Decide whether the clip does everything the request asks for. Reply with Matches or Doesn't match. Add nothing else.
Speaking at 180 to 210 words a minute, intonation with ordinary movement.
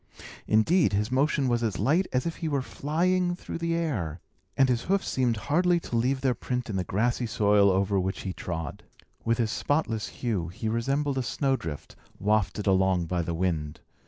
Doesn't match